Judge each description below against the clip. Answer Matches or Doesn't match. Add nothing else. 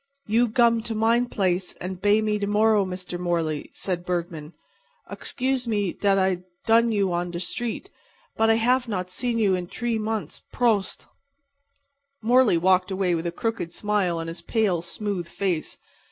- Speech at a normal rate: Matches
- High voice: Matches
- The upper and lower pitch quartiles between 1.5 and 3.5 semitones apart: Doesn't match